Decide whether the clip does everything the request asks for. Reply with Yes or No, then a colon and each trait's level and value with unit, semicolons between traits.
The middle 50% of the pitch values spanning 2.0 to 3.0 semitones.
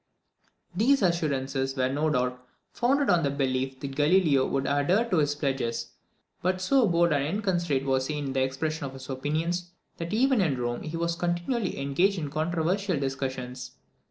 No: average, 4.8 semitones